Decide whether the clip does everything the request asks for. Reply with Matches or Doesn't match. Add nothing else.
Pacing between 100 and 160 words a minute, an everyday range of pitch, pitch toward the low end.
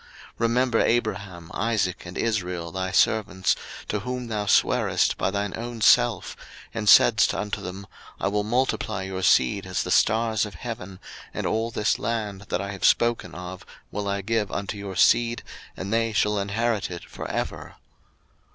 Doesn't match